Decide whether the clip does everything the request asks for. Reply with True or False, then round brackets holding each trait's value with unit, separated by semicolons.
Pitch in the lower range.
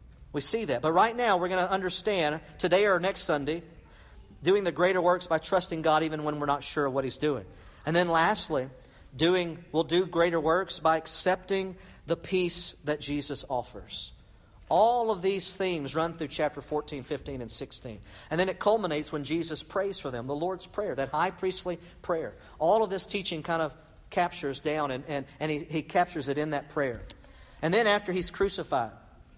False (160 Hz)